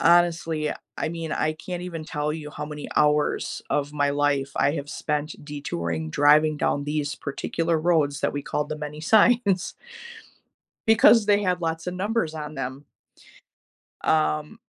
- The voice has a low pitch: No, medium, 155 Hz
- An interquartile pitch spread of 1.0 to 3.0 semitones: Yes, narrow, 2.6 semitones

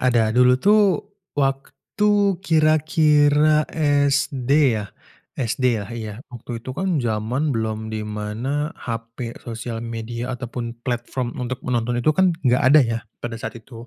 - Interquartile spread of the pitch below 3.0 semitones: No, average, 4.0 semitones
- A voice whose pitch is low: Yes, low, 125 Hz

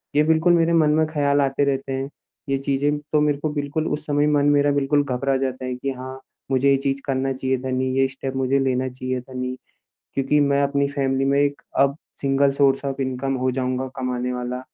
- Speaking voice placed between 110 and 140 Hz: Yes, low, 135 Hz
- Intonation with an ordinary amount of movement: No, narrow, 1.5 semitones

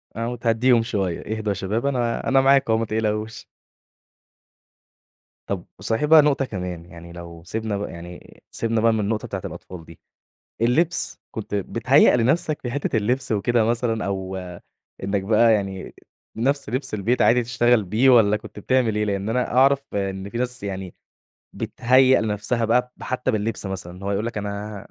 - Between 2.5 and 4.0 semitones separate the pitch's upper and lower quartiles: Yes, average, 3.7 semitones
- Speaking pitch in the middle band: No, low, 110 Hz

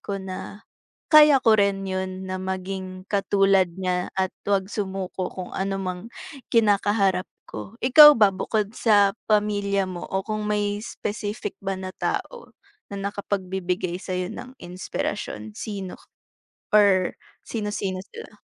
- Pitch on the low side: No, high, 195 Hz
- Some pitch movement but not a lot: No, narrow, 1.8 semitones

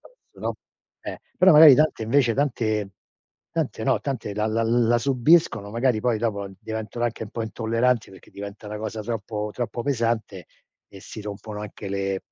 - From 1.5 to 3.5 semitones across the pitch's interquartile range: Yes, narrow, 2.5 semitones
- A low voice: Yes, low, 110 Hz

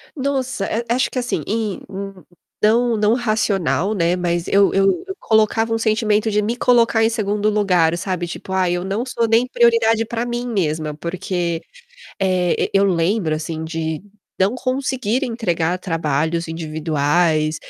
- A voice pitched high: Yes, high, 200 Hz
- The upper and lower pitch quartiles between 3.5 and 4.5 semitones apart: No, average, 5.1 semitones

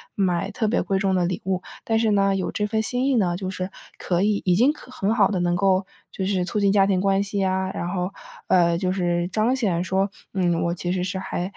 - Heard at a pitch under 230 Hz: Yes, high, 190 Hz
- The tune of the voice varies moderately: No, narrow, 2.2 semitones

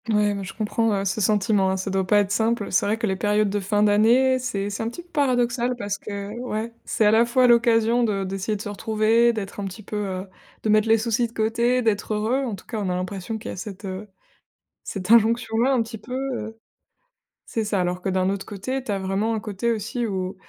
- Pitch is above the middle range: Yes, high, 215 Hz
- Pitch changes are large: No, average, 2.8 semitones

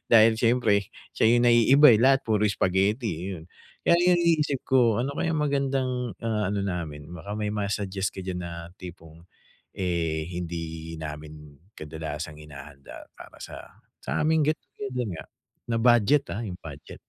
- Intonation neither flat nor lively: No, wide, 7.0 semitones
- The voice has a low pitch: Yes, low, 100 Hz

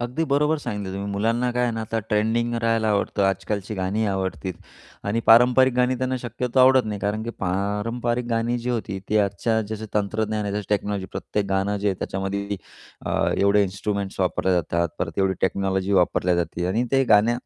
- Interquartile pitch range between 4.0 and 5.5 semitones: No, average, 3.2 semitones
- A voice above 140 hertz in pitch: No, low, 105 Hz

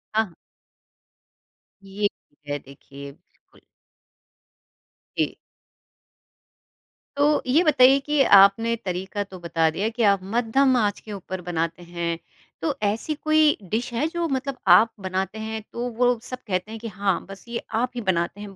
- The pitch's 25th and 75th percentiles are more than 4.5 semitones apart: Yes, average, 5.1 semitones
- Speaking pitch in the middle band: No, high, 215 Hz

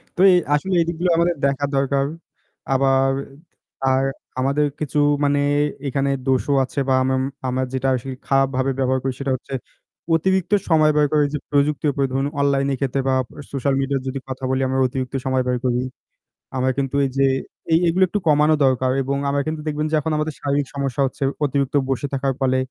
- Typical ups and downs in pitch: No, narrow, 1.9 semitones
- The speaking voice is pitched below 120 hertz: No, low, 135 Hz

